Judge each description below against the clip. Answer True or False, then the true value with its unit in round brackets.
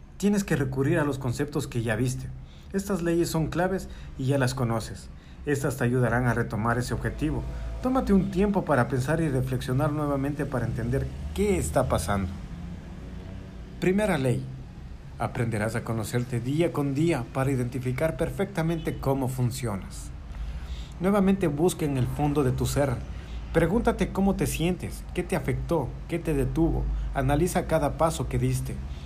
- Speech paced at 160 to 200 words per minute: False (150 wpm)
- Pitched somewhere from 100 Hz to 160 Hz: True (135 Hz)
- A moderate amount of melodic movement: False (5.8 semitones)